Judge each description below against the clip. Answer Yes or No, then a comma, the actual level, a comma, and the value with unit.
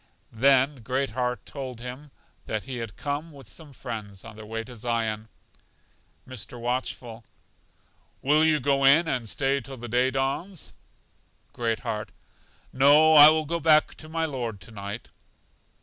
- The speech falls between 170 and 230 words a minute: No, average, 155 wpm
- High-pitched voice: No, low, 130 Hz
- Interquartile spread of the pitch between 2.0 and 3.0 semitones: No, average, 4.0 semitones